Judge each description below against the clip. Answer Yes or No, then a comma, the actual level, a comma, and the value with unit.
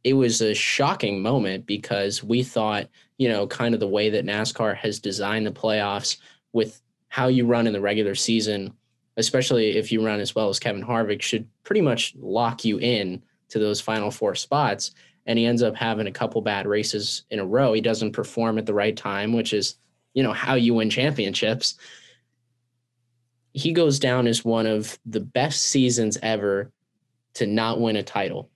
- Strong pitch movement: No, narrow, 2.4 semitones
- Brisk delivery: No, average, 190 wpm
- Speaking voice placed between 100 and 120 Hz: Yes, low, 110 Hz